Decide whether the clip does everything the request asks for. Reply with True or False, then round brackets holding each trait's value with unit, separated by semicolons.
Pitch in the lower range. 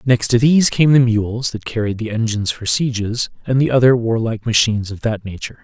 True (115 Hz)